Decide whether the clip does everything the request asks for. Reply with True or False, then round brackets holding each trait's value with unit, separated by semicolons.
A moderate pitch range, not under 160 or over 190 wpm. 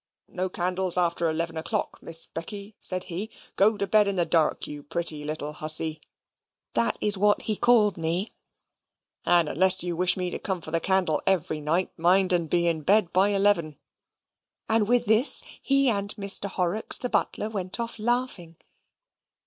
True (3.7 semitones; 175 wpm)